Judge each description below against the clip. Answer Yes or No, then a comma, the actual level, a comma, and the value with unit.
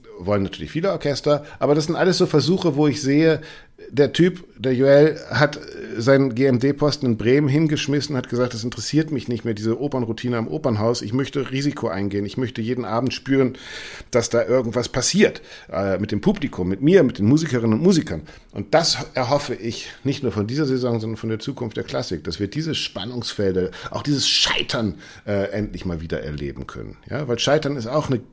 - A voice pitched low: Yes, low, 125 Hz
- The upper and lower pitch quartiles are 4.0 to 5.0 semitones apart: Yes, average, 4.4 semitones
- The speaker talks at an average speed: No, fast, 195 wpm